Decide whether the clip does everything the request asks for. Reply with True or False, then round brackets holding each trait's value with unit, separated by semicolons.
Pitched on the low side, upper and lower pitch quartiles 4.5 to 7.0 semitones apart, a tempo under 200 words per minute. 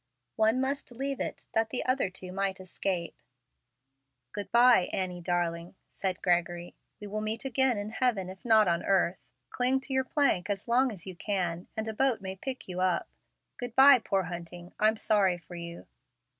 False (200 Hz; 5.2 semitones; 185 wpm)